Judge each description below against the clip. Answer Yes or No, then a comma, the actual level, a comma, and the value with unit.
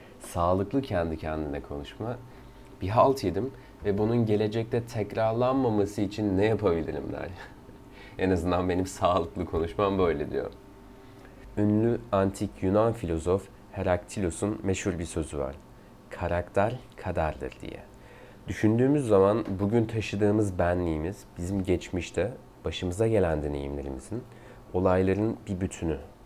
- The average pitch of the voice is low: Yes, low, 100 Hz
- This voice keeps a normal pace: Yes, average, 105 wpm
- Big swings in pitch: No, average, 4.0 semitones